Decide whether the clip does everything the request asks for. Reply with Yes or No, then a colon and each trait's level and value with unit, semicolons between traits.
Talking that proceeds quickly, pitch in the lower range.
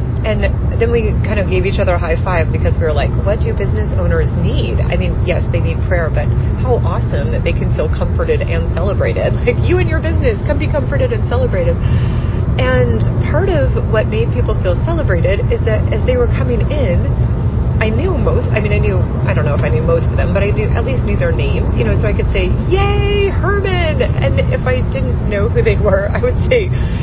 Yes: fast, 230 wpm; low, 110 Hz